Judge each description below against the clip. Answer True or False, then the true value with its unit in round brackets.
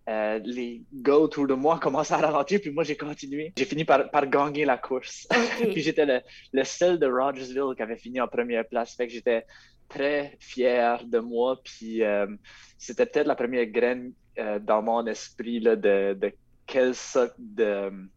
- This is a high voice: False (130 Hz)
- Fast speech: False (190 wpm)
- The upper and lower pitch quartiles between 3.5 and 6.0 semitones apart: True (4.1 semitones)